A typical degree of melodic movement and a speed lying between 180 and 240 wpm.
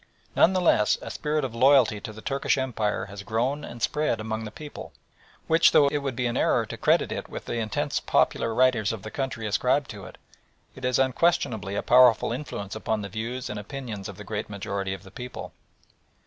Yes: average, 4.1 semitones; fast, 205 wpm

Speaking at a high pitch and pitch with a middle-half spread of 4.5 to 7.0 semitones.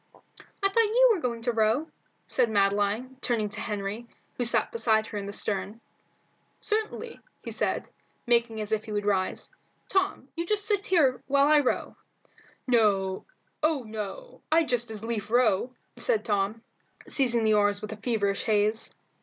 Yes: high, 230 Hz; wide, 5.4 semitones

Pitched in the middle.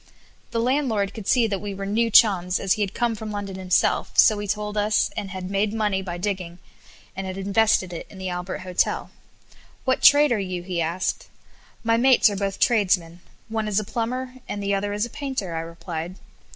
No: high, 200 Hz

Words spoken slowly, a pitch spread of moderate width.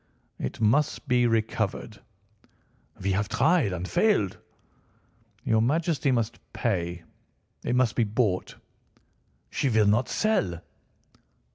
Yes: slow, 110 wpm; average, 4.6 semitones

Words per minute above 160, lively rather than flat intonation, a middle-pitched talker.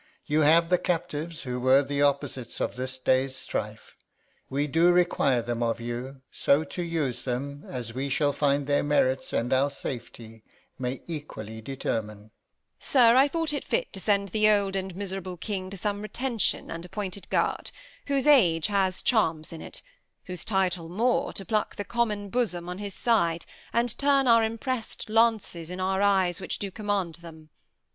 Yes: average, 175 wpm; wide, 6.6 semitones; medium, 175 Hz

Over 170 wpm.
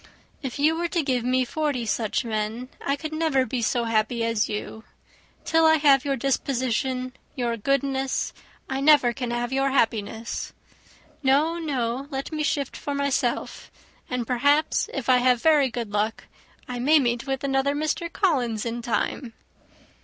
No: average, 160 wpm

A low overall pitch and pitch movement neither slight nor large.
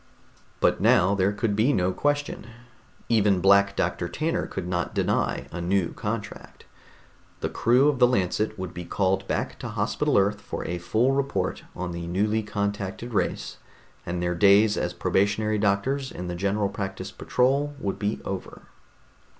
Yes: low, 100 Hz; average, 3.0 semitones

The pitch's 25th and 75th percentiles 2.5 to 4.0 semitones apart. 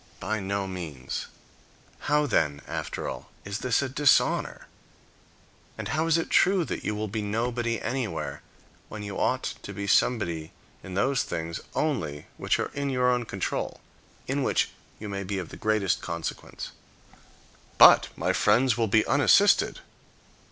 No: wide, 5.5 semitones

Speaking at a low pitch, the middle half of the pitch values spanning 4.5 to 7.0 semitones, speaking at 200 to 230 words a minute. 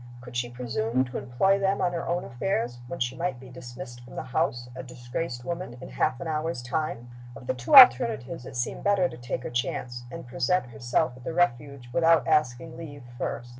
Yes: low, 125 Hz; average, 5.3 semitones; fast, 205 wpm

